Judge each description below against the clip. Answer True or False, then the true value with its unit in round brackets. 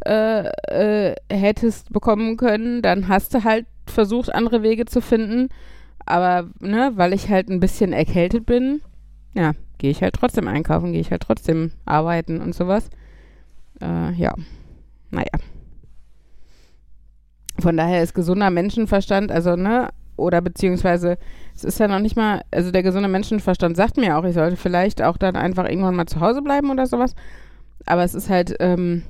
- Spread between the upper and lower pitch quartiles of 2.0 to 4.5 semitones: False (4.9 semitones)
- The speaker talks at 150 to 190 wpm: True (165 wpm)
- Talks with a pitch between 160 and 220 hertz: True (185 Hz)